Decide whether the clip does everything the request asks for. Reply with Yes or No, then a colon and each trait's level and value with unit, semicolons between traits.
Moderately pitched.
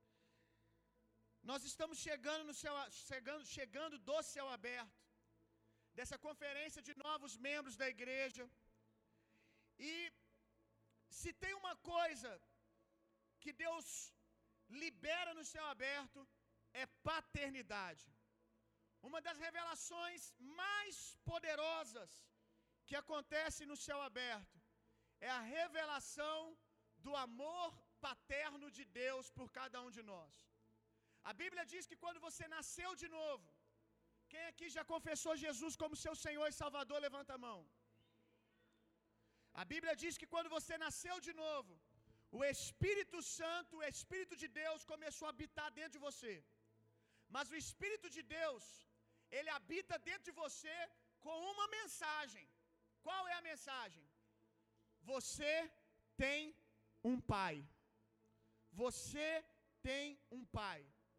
No: very high, 285 Hz